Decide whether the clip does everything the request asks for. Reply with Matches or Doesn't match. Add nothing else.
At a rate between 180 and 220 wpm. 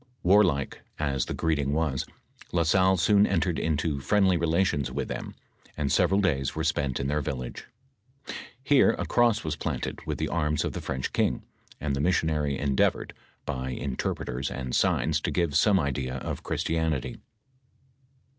Doesn't match